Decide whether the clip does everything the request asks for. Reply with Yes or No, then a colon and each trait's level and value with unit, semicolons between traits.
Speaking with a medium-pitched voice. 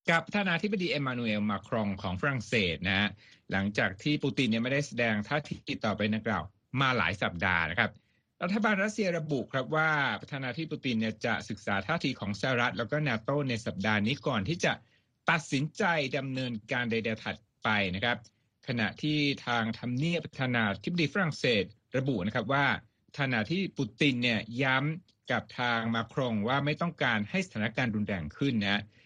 No: low, 125 Hz